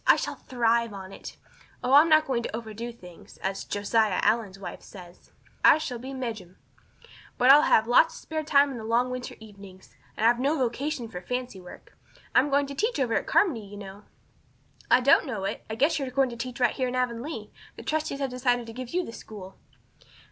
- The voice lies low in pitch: No, high, 240 Hz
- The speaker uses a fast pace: Yes, fast, 215 wpm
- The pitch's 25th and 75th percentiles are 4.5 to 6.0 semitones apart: No, average, 4.0 semitones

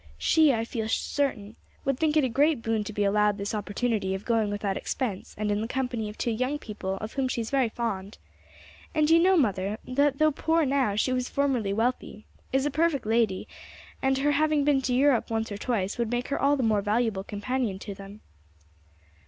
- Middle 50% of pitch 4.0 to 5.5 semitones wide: Yes, average, 4.7 semitones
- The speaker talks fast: Yes, fast, 210 wpm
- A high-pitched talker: Yes, high, 235 Hz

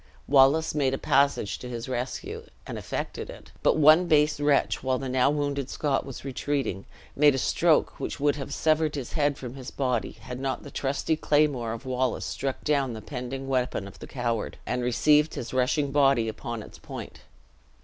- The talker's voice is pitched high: No, low, 135 Hz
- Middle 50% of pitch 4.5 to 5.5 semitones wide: No, average, 2.7 semitones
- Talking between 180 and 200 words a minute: Yes, average, 190 wpm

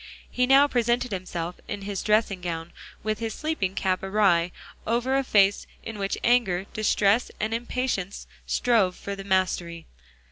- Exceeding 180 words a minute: No, average, 150 wpm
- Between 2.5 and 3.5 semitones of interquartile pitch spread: No, average, 4.1 semitones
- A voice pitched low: No, high, 205 Hz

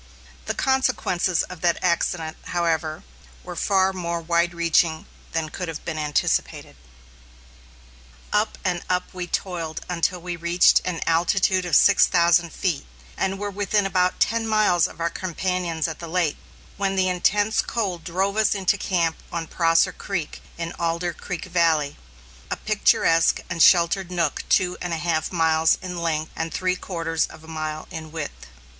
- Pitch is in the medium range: Yes, medium, 170 Hz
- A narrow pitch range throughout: Yes, narrow, 2.1 semitones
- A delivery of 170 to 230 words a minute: No, average, 160 wpm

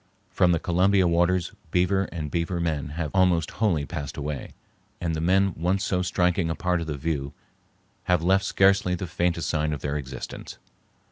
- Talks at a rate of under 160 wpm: No, average, 180 wpm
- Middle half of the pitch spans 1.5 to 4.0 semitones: Yes, average, 2.7 semitones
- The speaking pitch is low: Yes, very low, 85 Hz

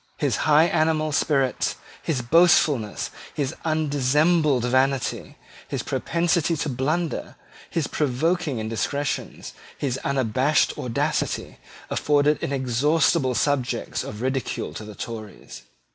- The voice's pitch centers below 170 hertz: Yes, medium, 140 Hz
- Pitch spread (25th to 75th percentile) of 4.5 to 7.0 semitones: No, average, 3.6 semitones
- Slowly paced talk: Yes, slow, 100 wpm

